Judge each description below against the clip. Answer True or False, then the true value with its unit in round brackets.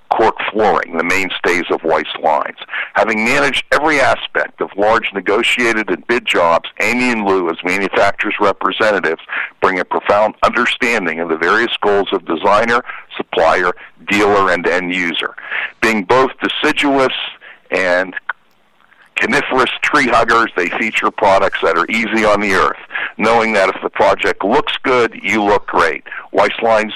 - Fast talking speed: False (145 wpm)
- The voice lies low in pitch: True (105 Hz)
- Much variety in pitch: False (3.2 semitones)